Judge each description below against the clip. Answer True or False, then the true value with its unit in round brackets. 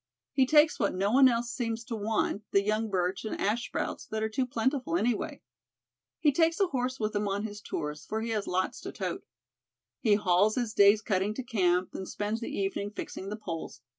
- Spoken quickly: True (210 wpm)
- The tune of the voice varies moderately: True (3.3 semitones)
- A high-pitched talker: True (215 Hz)